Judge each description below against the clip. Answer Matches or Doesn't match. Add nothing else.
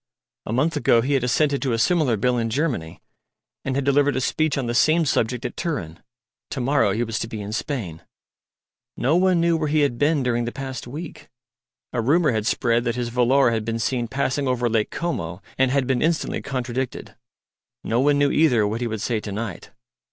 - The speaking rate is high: Matches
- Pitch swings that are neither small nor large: Matches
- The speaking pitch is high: Doesn't match